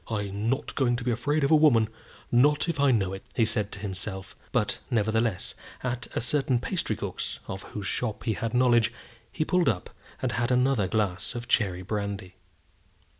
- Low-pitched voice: Yes, low, 115 Hz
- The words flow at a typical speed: Yes, average, 180 wpm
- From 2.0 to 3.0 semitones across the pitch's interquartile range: No, average, 3.8 semitones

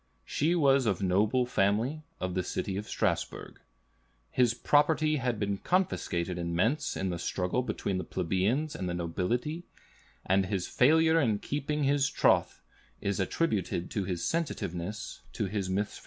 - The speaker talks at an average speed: Yes, average, 155 wpm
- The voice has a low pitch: Yes, low, 105 Hz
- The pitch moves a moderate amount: No, wide, 7.5 semitones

